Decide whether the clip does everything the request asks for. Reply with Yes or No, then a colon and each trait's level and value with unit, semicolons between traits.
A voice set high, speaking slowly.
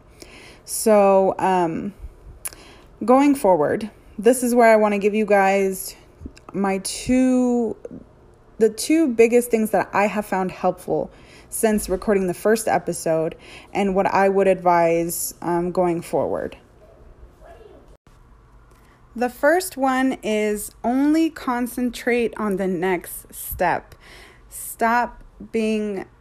Yes: high, 210 Hz; slow, 110 wpm